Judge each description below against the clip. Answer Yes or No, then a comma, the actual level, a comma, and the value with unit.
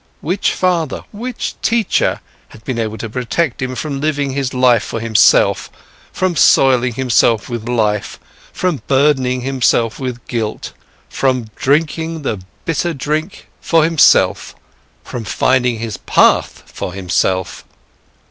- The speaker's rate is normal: No, slow, 130 wpm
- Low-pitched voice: Yes, low, 130 Hz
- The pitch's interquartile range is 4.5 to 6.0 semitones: Yes, average, 5.0 semitones